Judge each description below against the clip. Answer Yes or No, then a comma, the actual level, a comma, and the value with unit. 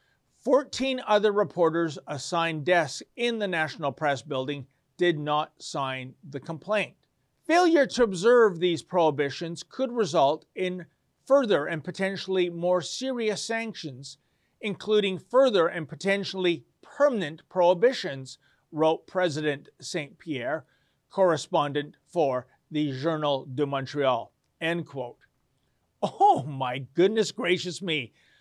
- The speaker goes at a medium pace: No, slow, 110 wpm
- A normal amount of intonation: No, wide, 5.7 semitones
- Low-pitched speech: No, medium, 170 Hz